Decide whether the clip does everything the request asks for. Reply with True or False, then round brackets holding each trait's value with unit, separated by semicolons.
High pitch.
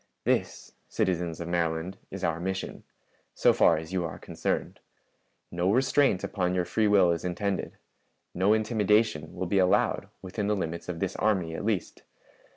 False (95 Hz)